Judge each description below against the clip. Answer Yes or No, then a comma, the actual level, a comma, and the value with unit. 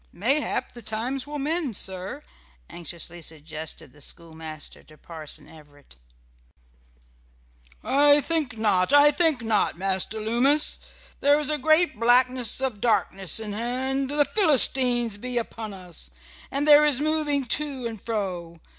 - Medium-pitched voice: No, high, 240 Hz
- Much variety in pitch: Yes, wide, 7.4 semitones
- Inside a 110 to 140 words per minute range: Yes, slow, 135 wpm